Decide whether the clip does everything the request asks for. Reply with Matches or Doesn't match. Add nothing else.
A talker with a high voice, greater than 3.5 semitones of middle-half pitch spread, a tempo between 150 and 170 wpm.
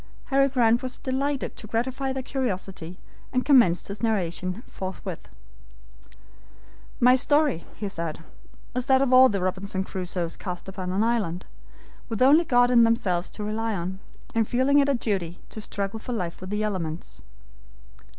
Matches